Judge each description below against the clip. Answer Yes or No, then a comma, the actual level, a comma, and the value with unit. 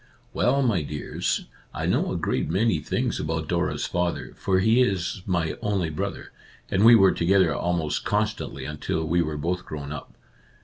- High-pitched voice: No, very low, 90 Hz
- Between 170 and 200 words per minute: Yes, average, 180 wpm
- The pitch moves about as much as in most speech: Yes, average, 4.0 semitones